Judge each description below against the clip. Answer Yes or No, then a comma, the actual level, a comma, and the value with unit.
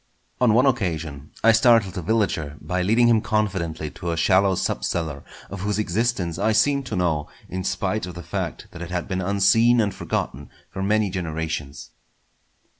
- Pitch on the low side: Yes, very low, 95 Hz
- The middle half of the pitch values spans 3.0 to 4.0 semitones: No, average, 4.5 semitones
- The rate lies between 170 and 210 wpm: Yes, average, 180 wpm